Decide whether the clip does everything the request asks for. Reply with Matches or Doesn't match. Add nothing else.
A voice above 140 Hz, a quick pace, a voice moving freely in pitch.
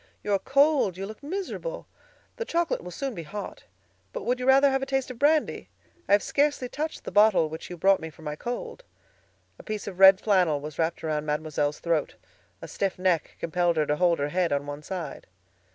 Matches